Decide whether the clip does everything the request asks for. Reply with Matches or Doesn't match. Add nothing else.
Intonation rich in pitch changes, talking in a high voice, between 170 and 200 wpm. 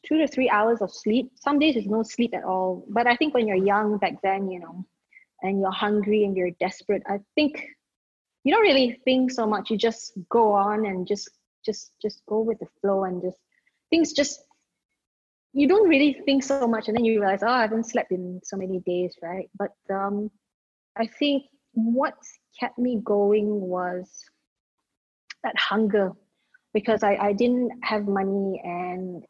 Doesn't match